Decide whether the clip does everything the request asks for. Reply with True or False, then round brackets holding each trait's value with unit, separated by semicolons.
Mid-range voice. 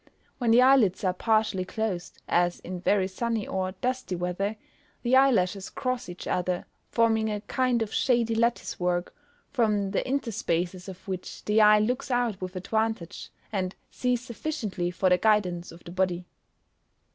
False (210 Hz)